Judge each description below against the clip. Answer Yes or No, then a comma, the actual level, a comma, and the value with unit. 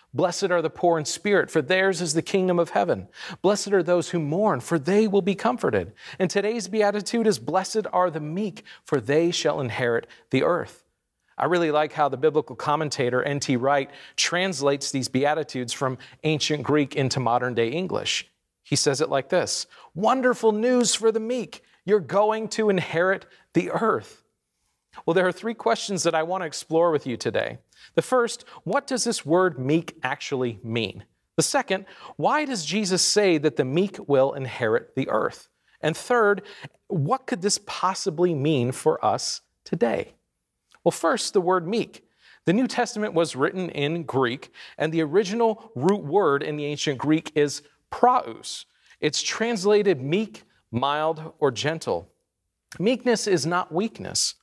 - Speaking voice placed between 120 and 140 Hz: No, medium, 175 Hz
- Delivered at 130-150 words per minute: No, average, 165 wpm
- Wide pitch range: Yes, wide, 5.8 semitones